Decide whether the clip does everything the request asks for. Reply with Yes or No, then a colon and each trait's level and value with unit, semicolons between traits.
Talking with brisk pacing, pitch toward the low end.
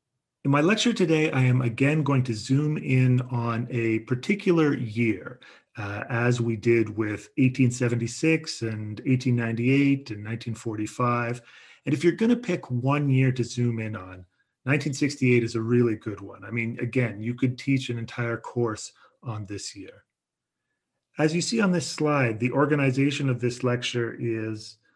No: average, 160 wpm; low, 125 Hz